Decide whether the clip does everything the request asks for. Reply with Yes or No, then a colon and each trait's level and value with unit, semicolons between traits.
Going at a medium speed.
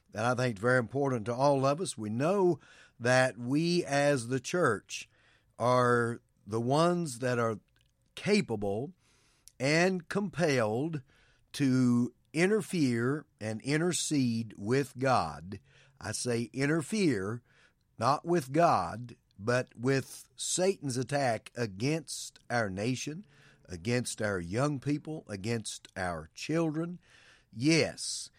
No: slow, 110 wpm